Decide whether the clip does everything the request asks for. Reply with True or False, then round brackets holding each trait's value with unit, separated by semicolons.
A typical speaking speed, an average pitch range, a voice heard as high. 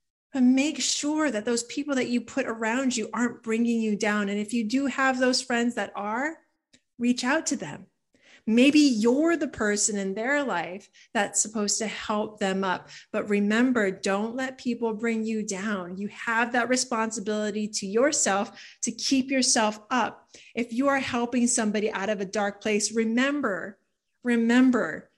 True (170 wpm; 3.7 semitones; 230 Hz)